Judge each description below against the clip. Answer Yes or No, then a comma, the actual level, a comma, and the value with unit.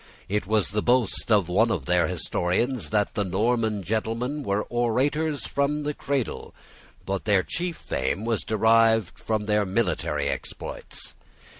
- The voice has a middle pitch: No, low, 110 Hz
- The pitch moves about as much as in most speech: Yes, average, 3.8 semitones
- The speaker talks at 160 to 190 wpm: No, average, 145 wpm